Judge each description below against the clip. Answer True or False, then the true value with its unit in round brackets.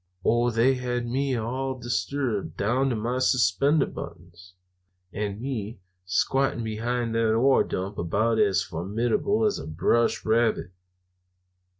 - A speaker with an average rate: False (125 wpm)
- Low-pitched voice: True (115 Hz)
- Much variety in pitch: False (3.9 semitones)